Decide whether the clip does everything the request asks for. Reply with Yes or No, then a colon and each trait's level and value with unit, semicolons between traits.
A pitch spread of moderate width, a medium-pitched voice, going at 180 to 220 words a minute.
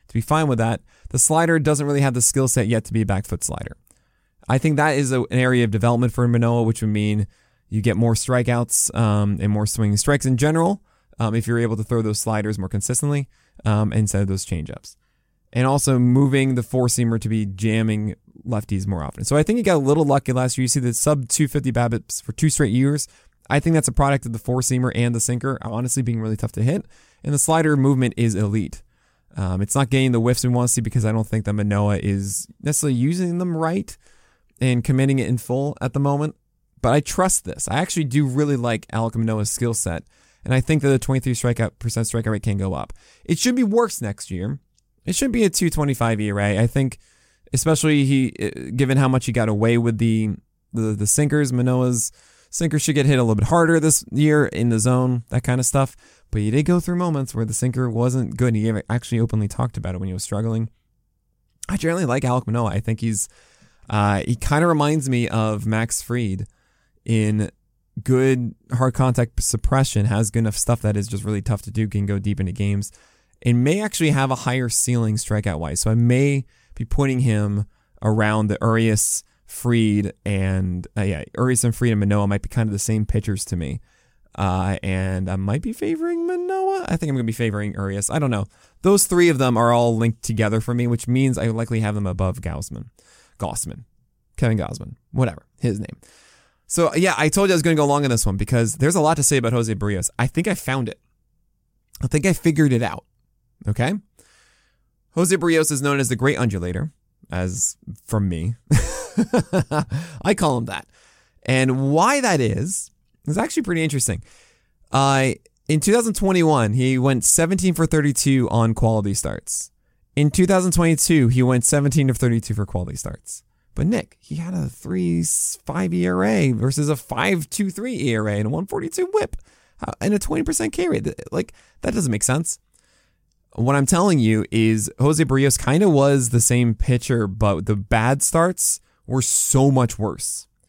No: average, 5.0 semitones; low, 120 Hz; fast, 205 wpm